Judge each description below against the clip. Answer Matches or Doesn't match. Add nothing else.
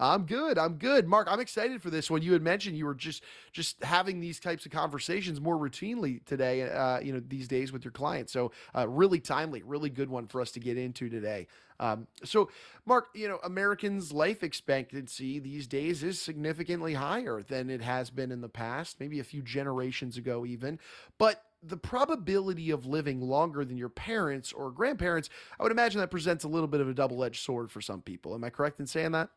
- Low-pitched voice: Doesn't match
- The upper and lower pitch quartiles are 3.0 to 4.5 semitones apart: Doesn't match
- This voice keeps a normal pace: Doesn't match